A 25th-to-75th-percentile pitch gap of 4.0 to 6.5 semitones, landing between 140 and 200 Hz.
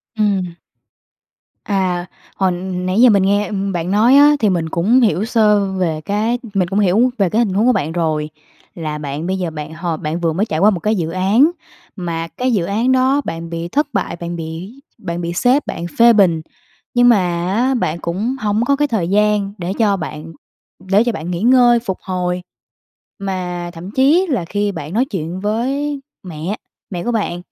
Yes: average, 4.8 semitones; high, 195 Hz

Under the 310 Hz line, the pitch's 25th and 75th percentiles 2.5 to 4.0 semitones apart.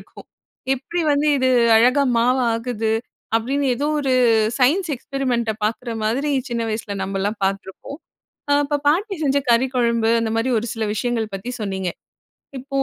Yes: high, 240 Hz; average, 3.6 semitones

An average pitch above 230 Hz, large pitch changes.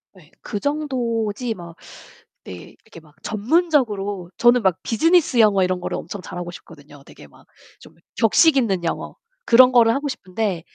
No: high, 215 Hz; wide, 5.7 semitones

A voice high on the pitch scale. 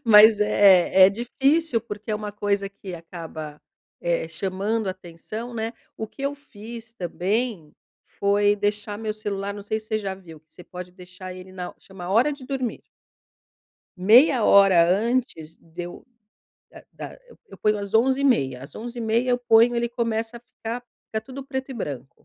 Yes: high, 210 Hz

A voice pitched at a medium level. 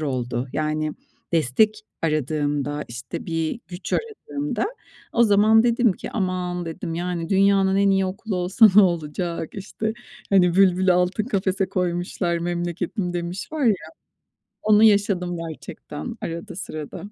Yes: medium, 180 Hz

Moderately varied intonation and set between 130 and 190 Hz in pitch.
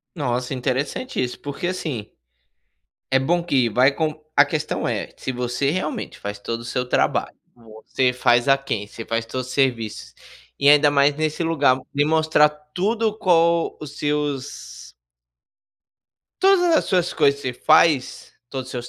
Yes: average, 4.0 semitones; medium, 140 Hz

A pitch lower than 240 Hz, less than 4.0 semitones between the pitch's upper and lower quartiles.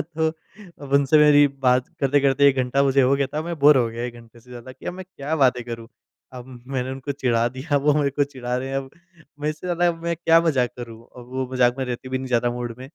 Yes: low, 135 Hz; average, 2.7 semitones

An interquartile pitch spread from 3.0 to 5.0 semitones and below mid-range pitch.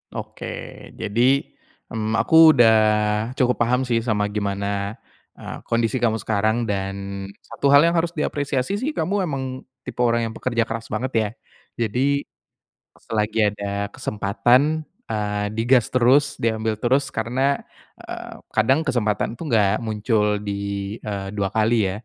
Yes: average, 3.5 semitones; low, 115 Hz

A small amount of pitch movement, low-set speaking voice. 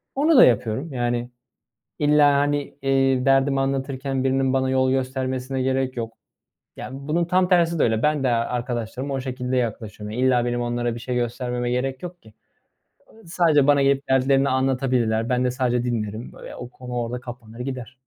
Yes: narrow, 2.0 semitones; low, 130 Hz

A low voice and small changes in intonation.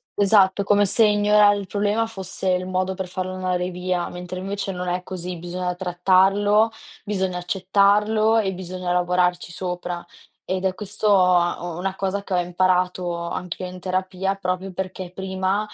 No: medium, 185 Hz; narrow, 1.7 semitones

